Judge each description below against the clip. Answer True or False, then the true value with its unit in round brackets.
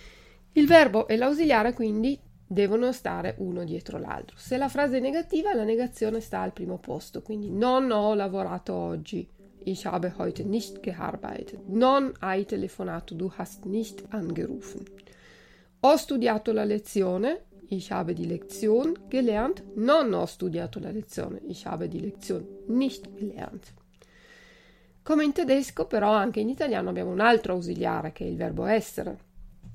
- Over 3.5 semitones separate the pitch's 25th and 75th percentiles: True (4.5 semitones)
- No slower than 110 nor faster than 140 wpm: False (150 wpm)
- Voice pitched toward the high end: True (215 Hz)